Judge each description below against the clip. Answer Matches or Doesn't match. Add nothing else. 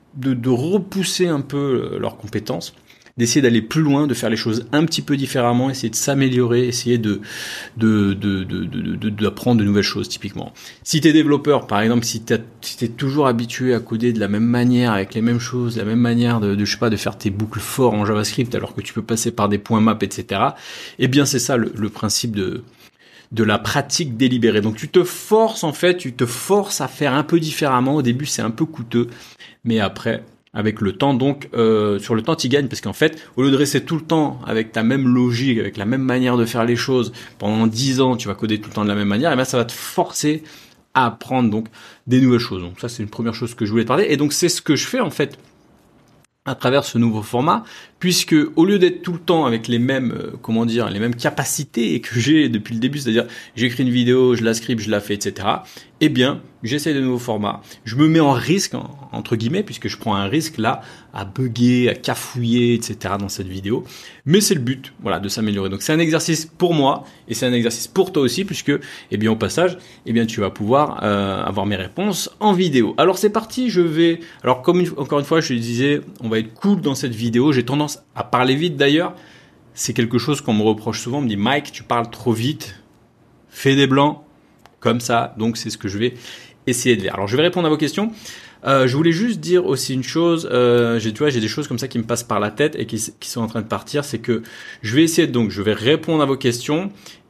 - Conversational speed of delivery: Doesn't match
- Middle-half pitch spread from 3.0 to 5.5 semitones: Matches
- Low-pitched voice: Matches